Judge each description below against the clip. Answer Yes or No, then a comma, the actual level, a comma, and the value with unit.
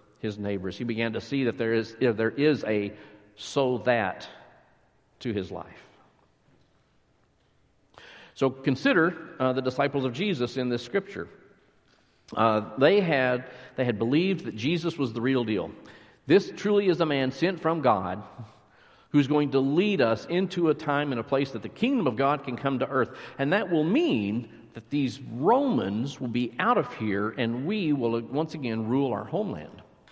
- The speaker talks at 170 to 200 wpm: Yes, average, 175 wpm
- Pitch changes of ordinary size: Yes, average, 4.2 semitones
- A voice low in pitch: Yes, low, 130 Hz